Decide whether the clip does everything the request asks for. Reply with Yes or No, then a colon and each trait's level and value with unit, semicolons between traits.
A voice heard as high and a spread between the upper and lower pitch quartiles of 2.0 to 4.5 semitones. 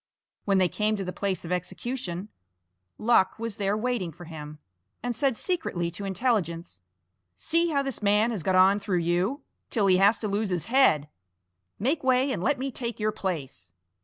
No: high, 200 Hz; average, 5.3 semitones